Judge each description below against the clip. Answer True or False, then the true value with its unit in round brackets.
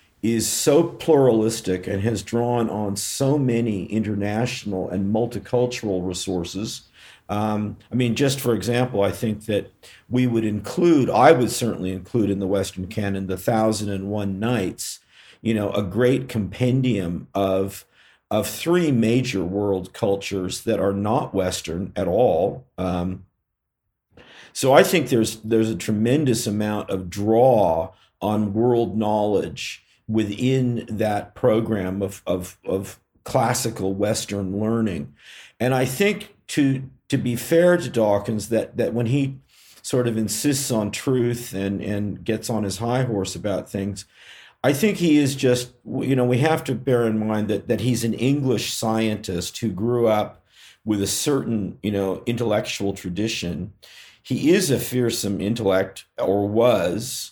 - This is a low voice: True (110 Hz)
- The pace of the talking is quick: False (145 wpm)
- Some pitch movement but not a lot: True (3.7 semitones)